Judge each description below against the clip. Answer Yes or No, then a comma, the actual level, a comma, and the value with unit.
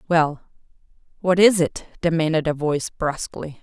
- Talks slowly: Yes, slow, 130 wpm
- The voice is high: No, medium, 165 Hz